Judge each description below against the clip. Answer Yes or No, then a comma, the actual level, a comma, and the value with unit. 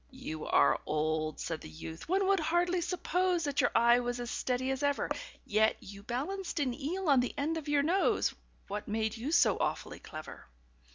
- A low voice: No, very high, 260 Hz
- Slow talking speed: No, average, 190 wpm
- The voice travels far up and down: Yes, wide, 7.3 semitones